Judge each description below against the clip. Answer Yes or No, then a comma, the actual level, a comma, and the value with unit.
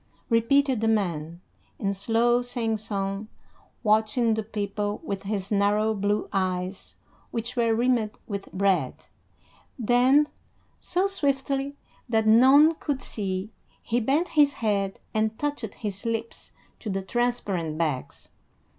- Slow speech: Yes, slow, 120 wpm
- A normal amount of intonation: Yes, average, 3.6 semitones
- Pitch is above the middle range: Yes, high, 220 Hz